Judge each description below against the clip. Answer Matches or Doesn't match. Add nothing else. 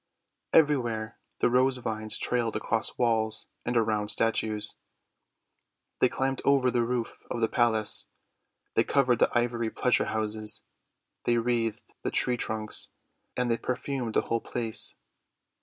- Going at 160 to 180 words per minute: Doesn't match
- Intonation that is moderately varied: Doesn't match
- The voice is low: Matches